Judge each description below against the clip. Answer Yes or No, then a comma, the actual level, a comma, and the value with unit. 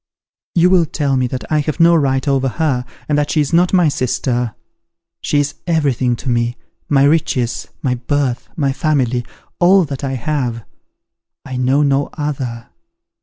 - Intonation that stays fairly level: No, average, 3.4 semitones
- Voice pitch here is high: No, medium, 140 Hz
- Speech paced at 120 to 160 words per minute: No, average, 170 wpm